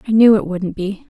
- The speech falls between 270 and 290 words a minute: No, fast, 255 wpm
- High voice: Yes, high, 205 Hz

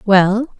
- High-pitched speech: Yes, high, 215 Hz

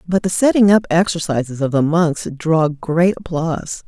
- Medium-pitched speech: Yes, medium, 165 Hz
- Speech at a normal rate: Yes, average, 170 wpm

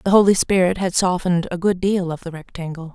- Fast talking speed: Yes, fast, 225 wpm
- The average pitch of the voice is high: No, medium, 180 Hz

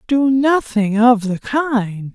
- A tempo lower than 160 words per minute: Yes, average, 140 wpm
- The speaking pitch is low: No, high, 235 Hz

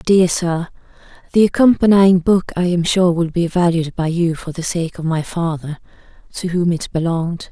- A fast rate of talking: No, average, 175 wpm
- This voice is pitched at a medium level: Yes, medium, 170 Hz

